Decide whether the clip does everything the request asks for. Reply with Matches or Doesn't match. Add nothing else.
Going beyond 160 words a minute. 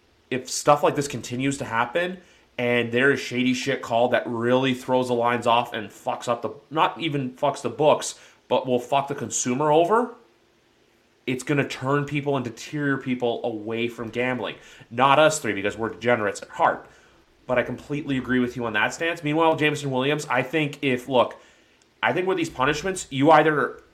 Matches